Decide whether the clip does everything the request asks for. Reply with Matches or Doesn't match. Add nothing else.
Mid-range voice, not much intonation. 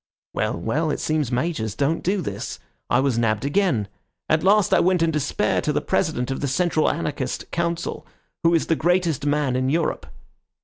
Doesn't match